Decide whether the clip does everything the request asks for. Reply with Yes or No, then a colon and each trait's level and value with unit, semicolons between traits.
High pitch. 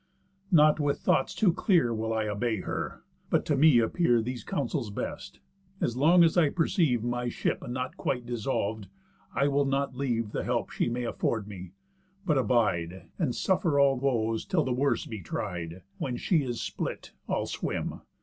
No: low, 125 Hz